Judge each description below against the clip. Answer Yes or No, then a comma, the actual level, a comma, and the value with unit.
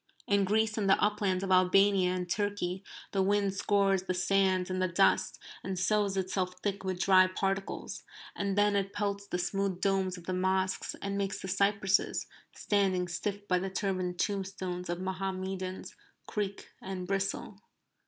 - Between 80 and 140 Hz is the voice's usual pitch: No, high, 195 Hz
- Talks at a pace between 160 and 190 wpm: Yes, average, 165 wpm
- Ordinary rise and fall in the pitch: No, narrow, 1.3 semitones